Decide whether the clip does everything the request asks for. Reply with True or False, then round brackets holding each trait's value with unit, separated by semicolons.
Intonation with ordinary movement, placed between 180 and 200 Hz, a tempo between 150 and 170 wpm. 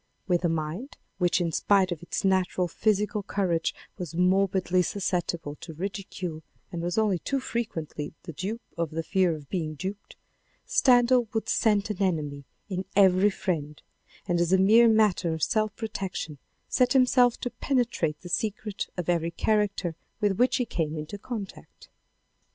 True (4.1 semitones; 190 Hz; 160 wpm)